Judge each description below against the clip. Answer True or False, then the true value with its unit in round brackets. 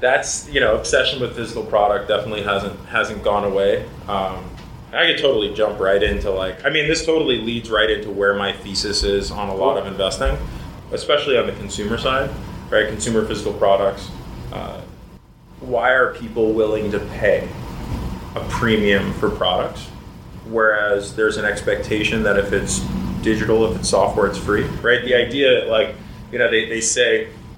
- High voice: False (110 Hz)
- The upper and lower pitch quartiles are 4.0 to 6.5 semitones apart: False (2.7 semitones)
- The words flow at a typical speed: True (170 wpm)